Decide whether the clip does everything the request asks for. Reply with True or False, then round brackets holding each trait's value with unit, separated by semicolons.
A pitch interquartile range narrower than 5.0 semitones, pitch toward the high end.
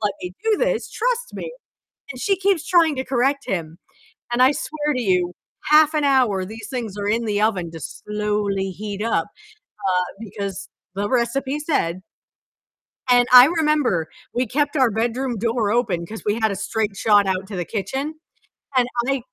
False (5.5 semitones; 230 Hz)